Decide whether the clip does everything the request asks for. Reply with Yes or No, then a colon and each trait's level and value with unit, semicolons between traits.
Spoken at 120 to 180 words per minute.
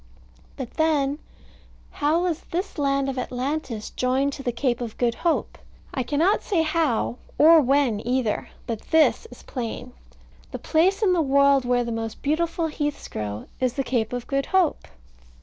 Yes: average, 165 wpm